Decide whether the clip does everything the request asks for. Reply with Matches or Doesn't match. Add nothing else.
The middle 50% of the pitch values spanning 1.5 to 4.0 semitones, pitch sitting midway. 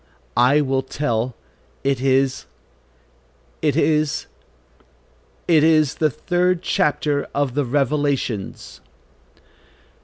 Matches